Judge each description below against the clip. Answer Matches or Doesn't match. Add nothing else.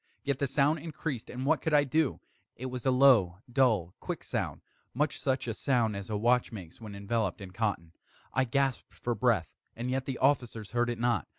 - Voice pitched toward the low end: Matches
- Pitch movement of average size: Matches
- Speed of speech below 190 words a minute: Doesn't match